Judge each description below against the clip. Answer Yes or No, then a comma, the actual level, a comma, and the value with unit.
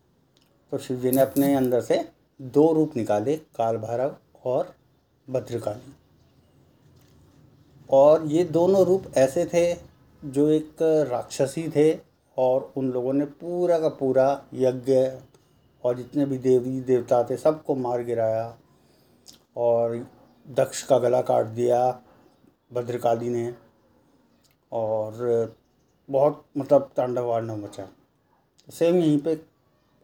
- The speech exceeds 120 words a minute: No, average, 115 wpm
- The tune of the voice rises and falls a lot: No, average, 3.7 semitones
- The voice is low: Yes, low, 130 Hz